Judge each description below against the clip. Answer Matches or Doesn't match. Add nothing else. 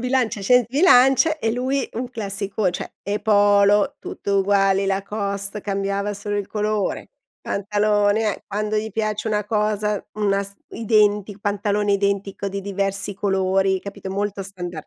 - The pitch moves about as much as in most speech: Doesn't match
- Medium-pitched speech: Doesn't match